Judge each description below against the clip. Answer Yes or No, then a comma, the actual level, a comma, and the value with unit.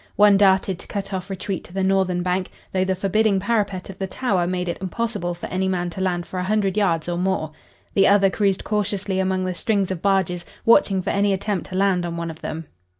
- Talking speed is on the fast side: Yes, fast, 230 wpm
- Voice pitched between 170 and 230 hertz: Yes, high, 190 Hz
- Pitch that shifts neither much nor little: No, narrow, 1.8 semitones